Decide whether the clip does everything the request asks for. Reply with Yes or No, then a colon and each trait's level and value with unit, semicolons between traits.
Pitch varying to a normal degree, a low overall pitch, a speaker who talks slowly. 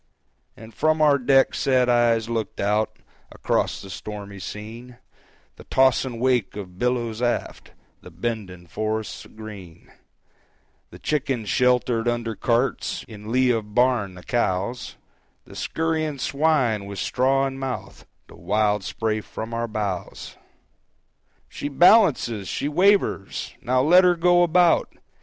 Yes: average, 4.1 semitones; low, 120 Hz; slow, 130 wpm